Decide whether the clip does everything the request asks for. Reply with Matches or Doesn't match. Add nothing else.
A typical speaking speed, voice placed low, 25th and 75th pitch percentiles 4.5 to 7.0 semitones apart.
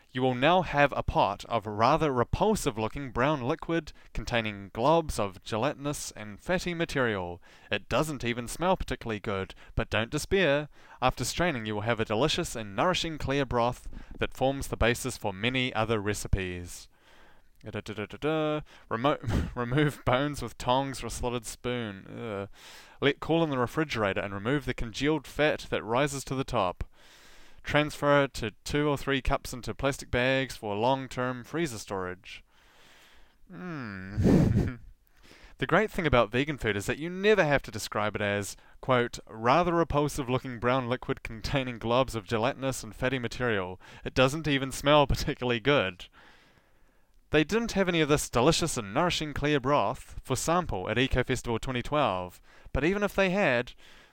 Matches